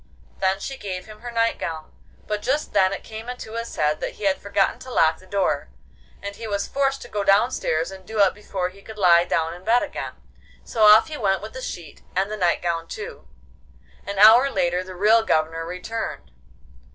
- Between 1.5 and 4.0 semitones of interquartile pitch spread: Yes, average, 3.7 semitones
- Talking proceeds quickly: Yes, fast, 215 wpm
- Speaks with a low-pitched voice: No, high, 200 Hz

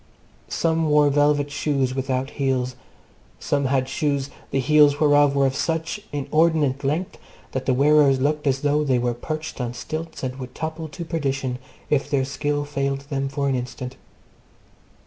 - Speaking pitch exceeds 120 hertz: Yes, medium, 140 Hz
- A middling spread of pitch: No, narrow, 2.1 semitones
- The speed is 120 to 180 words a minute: Yes, average, 160 wpm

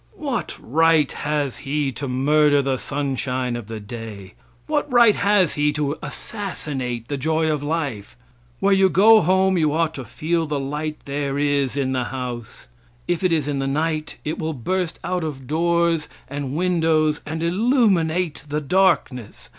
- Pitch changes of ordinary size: Yes, average, 3.8 semitones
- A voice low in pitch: No, medium, 150 Hz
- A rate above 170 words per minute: No, average, 165 wpm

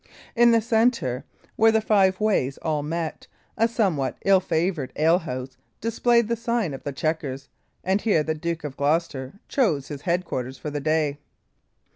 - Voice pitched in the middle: Yes, medium, 165 Hz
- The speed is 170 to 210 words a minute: No, average, 160 wpm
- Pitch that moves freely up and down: Yes, wide, 7.0 semitones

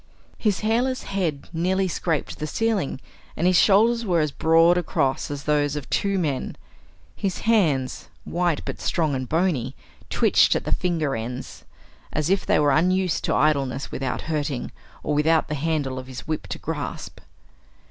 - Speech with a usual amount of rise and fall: Yes, average, 4.6 semitones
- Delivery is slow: No, average, 165 wpm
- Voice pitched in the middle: Yes, medium, 160 Hz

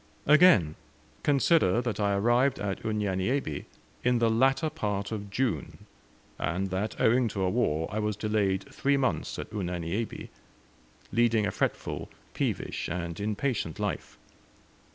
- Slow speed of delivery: Yes, slow, 130 wpm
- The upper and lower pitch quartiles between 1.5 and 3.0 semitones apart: No, average, 4.3 semitones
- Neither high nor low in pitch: No, low, 105 Hz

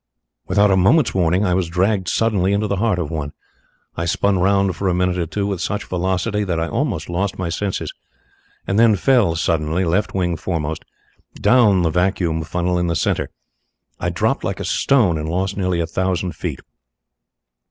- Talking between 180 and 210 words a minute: Yes, average, 185 wpm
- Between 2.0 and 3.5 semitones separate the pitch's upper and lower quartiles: Yes, average, 2.8 semitones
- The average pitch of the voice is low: Yes, very low, 90 Hz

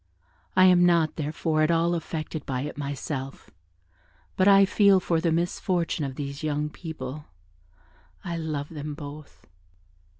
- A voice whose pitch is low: No, medium, 155 Hz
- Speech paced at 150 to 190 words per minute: No, average, 140 wpm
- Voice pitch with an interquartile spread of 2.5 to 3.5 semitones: Yes, average, 2.8 semitones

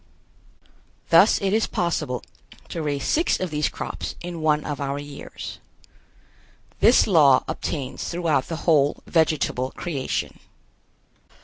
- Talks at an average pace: No, slow, 120 wpm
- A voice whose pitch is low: No, medium, 155 Hz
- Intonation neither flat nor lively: Yes, average, 3.4 semitones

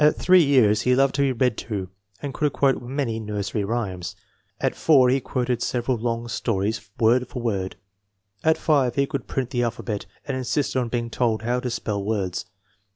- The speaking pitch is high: No, low, 120 Hz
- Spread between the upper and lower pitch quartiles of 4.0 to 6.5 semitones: No, average, 3.3 semitones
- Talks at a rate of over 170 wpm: Yes, average, 190 wpm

